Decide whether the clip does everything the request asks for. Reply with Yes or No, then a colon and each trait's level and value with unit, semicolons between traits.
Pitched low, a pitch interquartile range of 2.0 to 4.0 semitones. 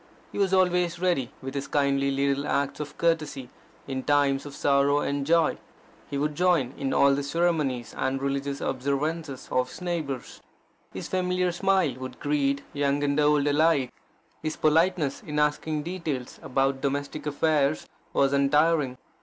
No: medium, 145 Hz; average, 2.7 semitones